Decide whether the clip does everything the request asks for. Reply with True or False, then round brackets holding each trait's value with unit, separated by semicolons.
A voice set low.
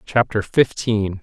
True (105 Hz)